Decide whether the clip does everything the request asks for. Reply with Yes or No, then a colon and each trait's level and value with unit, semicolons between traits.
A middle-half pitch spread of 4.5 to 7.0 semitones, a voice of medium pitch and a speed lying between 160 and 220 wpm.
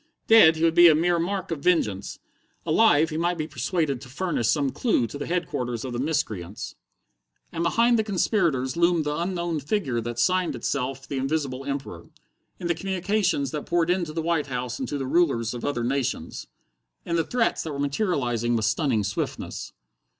Yes: average, 5.2 semitones; medium, 155 Hz; average, 190 wpm